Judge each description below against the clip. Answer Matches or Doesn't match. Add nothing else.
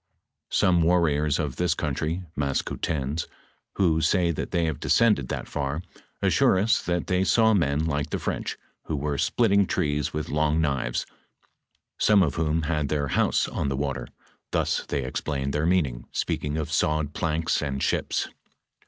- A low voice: Matches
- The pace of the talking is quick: Doesn't match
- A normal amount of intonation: Matches